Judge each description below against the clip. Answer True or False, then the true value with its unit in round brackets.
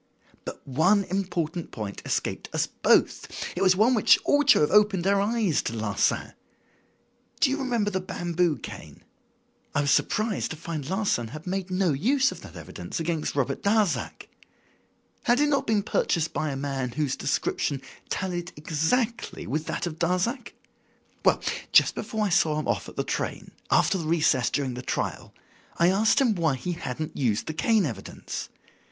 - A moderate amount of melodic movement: False (5.8 semitones)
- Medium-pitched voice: True (175 Hz)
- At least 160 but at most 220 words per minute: True (170 wpm)